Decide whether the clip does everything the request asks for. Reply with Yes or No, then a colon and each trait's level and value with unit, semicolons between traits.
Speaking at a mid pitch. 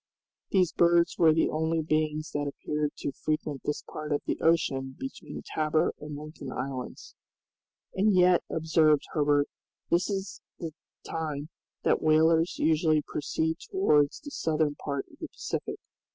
Yes: medium, 155 Hz